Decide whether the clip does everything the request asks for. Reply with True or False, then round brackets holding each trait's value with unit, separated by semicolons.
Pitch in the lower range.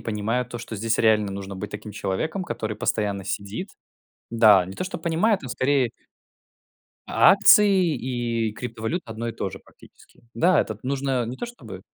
True (115 Hz)